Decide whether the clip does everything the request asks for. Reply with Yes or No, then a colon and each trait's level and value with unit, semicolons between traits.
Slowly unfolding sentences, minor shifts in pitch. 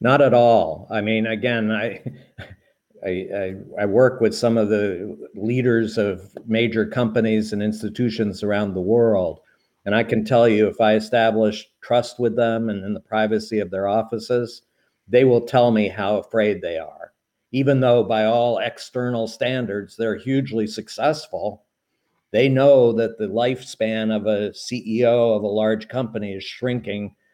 No: average, 160 wpm; narrow, 2.0 semitones